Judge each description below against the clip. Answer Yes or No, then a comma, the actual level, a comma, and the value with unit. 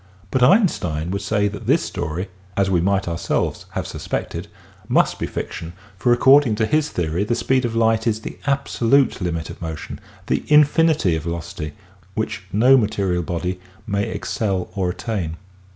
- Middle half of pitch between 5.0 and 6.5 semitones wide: Yes, wide, 5.4 semitones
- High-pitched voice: No, low, 100 Hz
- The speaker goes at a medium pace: Yes, average, 175 wpm